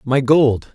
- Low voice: Yes, low, 130 Hz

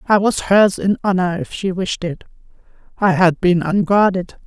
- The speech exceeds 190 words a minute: No, average, 175 wpm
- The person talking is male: No, female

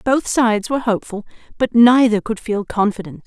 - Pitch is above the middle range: Yes, high, 225 Hz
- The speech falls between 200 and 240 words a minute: No, average, 165 wpm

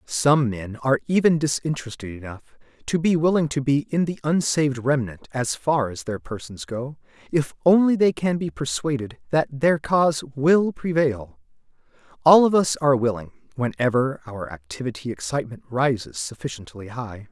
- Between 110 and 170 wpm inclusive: Yes, average, 150 wpm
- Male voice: Yes, male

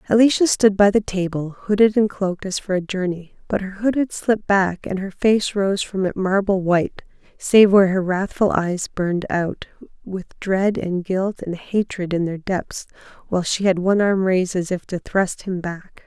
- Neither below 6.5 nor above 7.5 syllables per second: No, 4.8 syllables/s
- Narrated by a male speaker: No, female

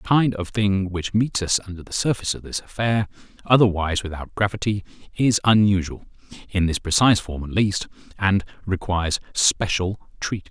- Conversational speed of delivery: Yes, average, 150 wpm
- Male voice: Yes, male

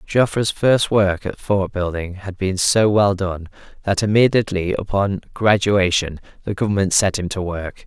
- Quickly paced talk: No, average, 160 wpm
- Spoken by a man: Yes, male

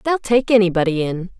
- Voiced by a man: No, female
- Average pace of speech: Yes, average, 170 wpm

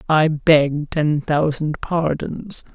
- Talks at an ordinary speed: No, slow, 110 wpm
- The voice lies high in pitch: No, medium, 155 Hz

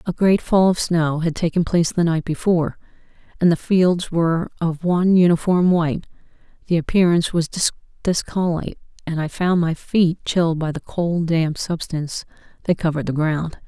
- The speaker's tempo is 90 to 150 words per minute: No, average, 165 wpm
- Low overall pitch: No, medium, 170 Hz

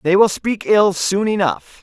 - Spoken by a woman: No, male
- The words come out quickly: No, average, 195 wpm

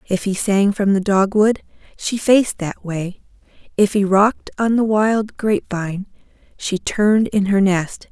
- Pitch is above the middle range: Yes, high, 200 Hz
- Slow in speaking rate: No, average, 170 wpm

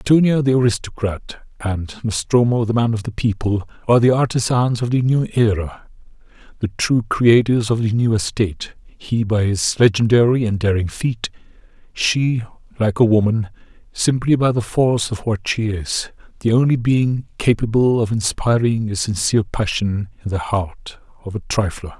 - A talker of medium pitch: No, low, 110 Hz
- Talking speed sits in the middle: Yes, average, 160 wpm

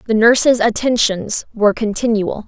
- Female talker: Yes, female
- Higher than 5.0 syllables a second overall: No, 4.9 syllables/s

